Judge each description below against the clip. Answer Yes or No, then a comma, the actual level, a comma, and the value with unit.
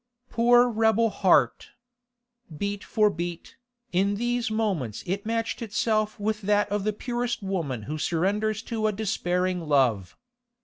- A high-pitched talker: Yes, high, 205 Hz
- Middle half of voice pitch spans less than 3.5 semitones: No, average, 3.9 semitones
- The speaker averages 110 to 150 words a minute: Yes, slow, 135 wpm